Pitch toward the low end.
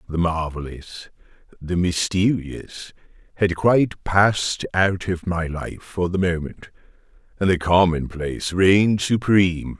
Yes: very low, 90 Hz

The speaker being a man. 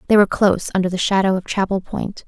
No: female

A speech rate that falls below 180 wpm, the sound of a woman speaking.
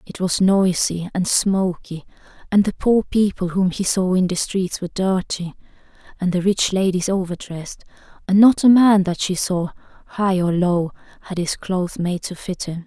No: average, 185 wpm; female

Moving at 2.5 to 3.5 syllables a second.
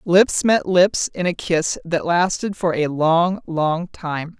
Yes: 3.4 syllables/s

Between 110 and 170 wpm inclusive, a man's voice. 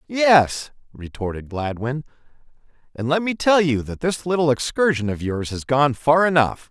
Yes: average, 160 wpm; male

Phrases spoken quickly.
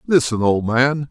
No: average, 160 wpm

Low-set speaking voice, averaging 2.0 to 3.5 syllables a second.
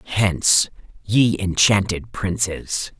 Yes: low, 100 Hz; 3.2 syllables/s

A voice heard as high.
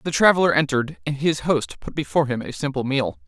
No: medium, 145 Hz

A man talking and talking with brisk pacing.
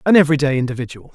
No: male; average, 155 wpm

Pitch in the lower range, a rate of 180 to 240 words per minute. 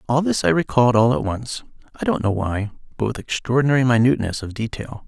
Yes: low, 115 Hz; average, 200 wpm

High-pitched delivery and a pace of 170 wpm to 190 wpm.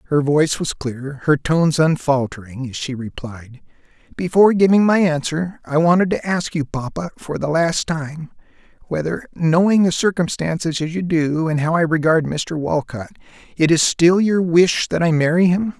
No: medium, 160 Hz; average, 175 wpm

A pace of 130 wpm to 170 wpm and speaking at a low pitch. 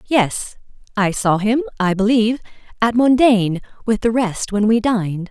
No: average, 160 wpm; high, 220 Hz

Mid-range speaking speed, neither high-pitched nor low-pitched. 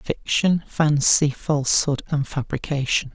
No: slow, 95 wpm; medium, 145 Hz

